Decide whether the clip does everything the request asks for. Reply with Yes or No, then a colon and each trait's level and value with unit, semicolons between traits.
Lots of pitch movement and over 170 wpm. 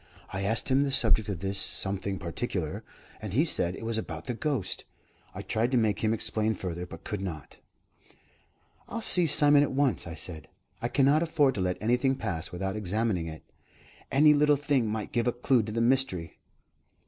Yes: wide, 6.0 semitones; average, 190 wpm